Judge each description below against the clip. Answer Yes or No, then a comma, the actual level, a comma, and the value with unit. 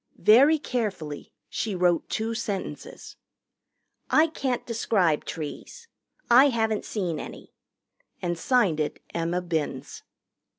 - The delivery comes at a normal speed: No, slow, 110 wpm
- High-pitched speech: Yes, high, 210 Hz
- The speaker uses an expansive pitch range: Yes, wide, 6.2 semitones